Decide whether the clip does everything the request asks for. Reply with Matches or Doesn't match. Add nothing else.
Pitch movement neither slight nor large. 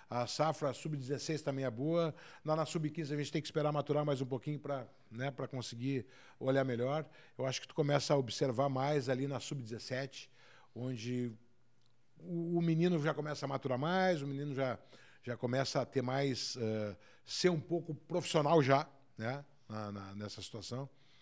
Matches